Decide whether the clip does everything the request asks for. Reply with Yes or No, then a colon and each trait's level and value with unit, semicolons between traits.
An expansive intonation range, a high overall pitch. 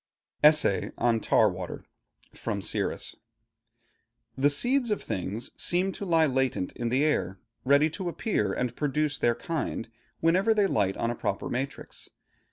No: wide, 6.3 semitones; medium, 140 Hz